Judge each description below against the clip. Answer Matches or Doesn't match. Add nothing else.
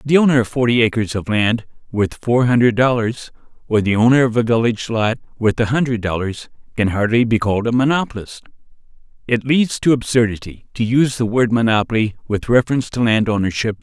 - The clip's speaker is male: Matches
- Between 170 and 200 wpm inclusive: Matches